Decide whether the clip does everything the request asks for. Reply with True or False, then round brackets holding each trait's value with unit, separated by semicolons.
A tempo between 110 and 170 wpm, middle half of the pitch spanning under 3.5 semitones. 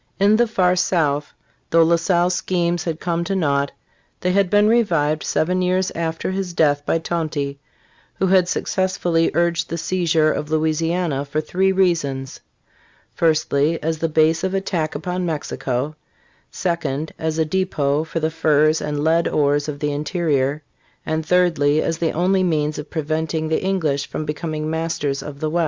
True (165 wpm; 2.9 semitones)